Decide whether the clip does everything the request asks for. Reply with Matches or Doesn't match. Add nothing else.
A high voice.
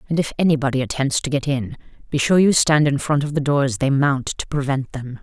Doesn't match